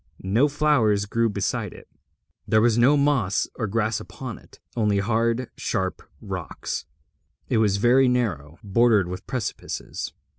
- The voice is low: Yes, low, 115 Hz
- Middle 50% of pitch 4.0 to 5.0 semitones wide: No, average, 3.6 semitones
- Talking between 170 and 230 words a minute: No, average, 140 wpm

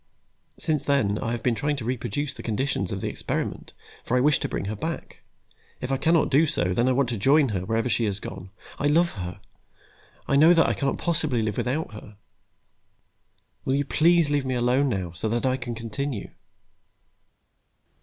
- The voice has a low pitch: Yes, low, 130 Hz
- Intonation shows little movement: No, average, 4.9 semitones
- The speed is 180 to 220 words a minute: Yes, average, 200 wpm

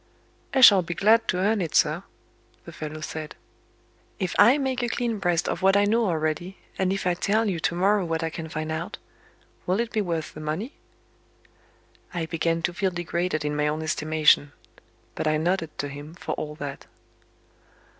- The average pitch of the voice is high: No, medium, 175 Hz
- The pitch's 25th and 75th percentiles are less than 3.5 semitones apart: No, average, 4.1 semitones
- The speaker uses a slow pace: No, average, 190 wpm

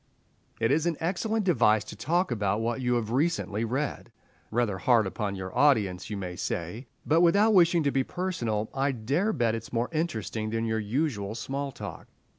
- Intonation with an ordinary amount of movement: No, wide, 6.5 semitones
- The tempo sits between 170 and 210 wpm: Yes, average, 190 wpm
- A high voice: No, low, 120 Hz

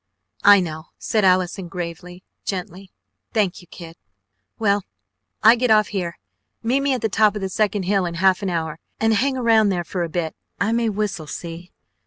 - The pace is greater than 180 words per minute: Yes, average, 190 wpm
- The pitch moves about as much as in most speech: Yes, average, 3.6 semitones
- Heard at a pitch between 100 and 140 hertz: No, high, 195 Hz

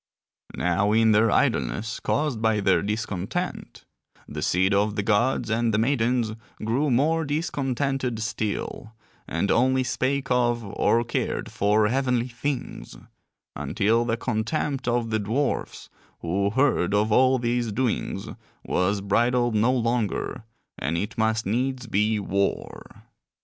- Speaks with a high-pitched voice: No, low, 115 Hz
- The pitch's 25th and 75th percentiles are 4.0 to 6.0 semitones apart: No, average, 3.4 semitones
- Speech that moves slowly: Yes, slow, 130 wpm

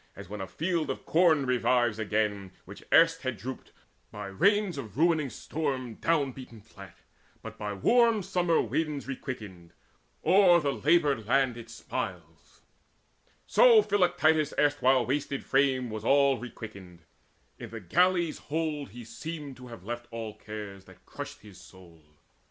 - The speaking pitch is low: Yes, low, 130 Hz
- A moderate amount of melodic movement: No, wide, 6.7 semitones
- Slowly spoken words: No, average, 145 wpm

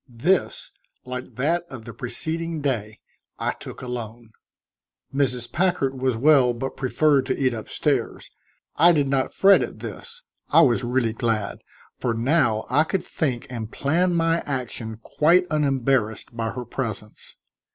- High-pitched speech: No, low, 130 Hz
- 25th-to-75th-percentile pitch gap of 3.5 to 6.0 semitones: Yes, average, 4.6 semitones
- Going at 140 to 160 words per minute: Yes, average, 150 wpm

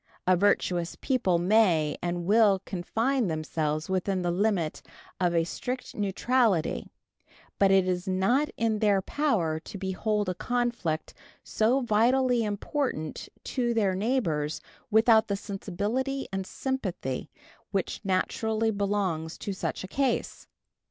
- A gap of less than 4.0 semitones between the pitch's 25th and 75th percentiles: No, average, 4.4 semitones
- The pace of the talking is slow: Yes, slow, 125 wpm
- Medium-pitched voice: No, high, 200 Hz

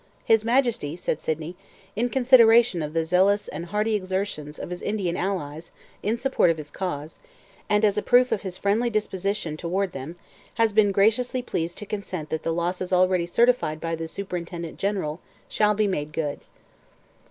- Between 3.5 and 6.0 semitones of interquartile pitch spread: Yes, average, 4.4 semitones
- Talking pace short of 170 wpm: No, average, 175 wpm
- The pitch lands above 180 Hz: Yes, high, 190 Hz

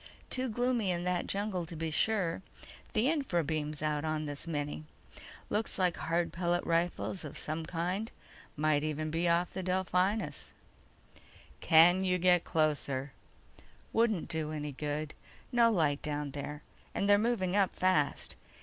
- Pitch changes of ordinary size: Yes, average, 3.6 semitones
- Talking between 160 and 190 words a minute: No, average, 150 wpm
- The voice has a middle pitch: Yes, medium, 170 Hz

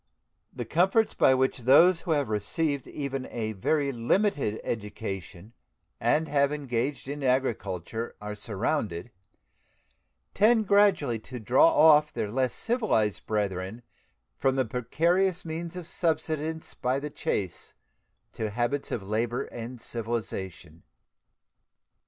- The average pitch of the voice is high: No, low, 130 Hz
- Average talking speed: No, slow, 120 wpm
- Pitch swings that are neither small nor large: No, wide, 6.2 semitones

